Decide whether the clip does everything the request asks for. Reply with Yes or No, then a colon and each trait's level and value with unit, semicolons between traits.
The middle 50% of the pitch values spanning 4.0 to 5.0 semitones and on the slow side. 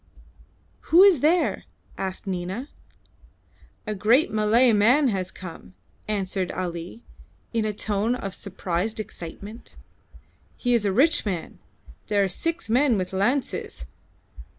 Yes: average, 4.6 semitones; slow, 125 wpm